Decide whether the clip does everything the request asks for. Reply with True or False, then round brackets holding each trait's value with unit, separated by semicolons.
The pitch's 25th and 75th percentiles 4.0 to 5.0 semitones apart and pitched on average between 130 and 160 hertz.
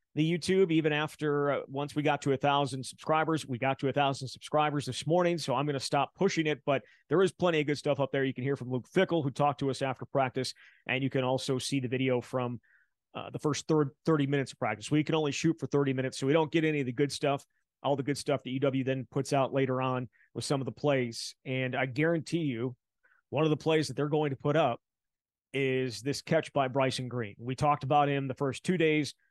False (2.6 semitones; 140 Hz)